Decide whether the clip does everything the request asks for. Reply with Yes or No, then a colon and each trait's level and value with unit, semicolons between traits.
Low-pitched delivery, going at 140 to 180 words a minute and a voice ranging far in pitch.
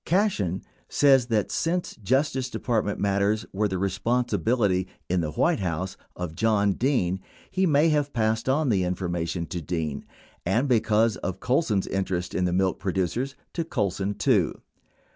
Yes: low, 105 Hz; average, 160 wpm; wide, 5.8 semitones